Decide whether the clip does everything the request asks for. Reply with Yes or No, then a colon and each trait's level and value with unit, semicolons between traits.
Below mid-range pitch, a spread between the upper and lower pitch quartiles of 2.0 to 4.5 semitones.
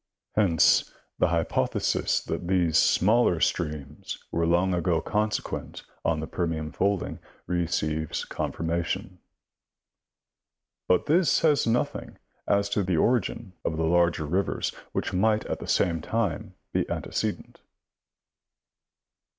Yes: very low, 85 Hz; average, 3.6 semitones